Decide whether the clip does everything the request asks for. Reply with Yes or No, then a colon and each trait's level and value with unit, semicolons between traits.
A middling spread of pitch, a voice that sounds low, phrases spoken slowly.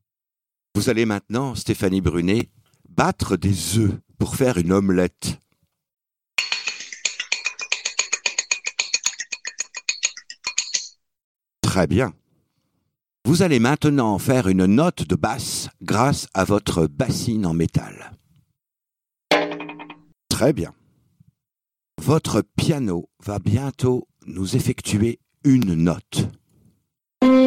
No: wide, 8.1 semitones; low, 115 Hz; slow, 85 wpm